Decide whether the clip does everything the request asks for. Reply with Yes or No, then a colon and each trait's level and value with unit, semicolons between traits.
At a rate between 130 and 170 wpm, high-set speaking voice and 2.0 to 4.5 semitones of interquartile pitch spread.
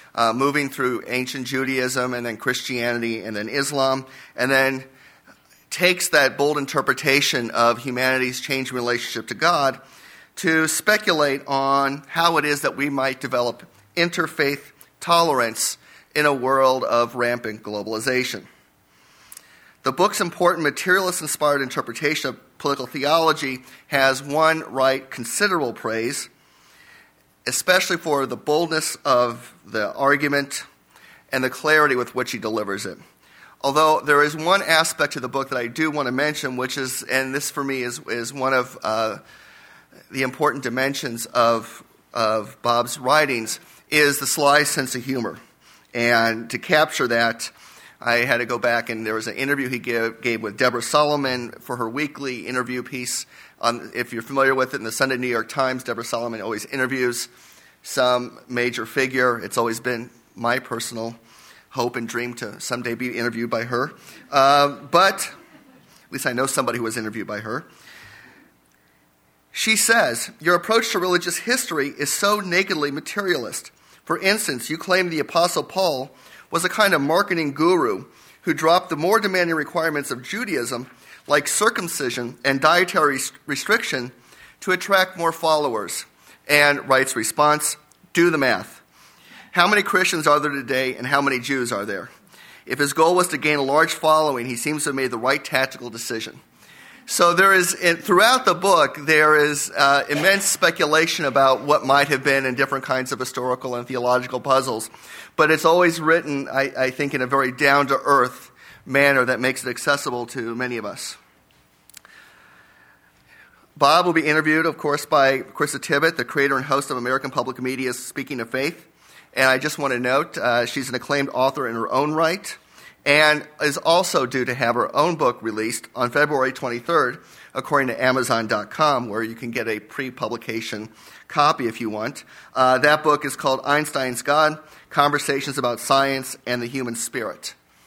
No: average, 165 wpm; low, 135 Hz; average, 3.5 semitones